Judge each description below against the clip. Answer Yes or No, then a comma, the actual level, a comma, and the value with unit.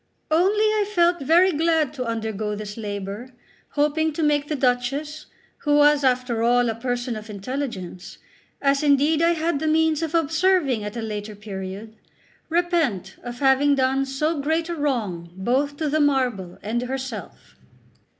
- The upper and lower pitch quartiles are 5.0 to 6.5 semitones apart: Yes, wide, 5.6 semitones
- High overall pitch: Yes, very high, 270 Hz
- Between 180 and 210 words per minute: No, average, 160 wpm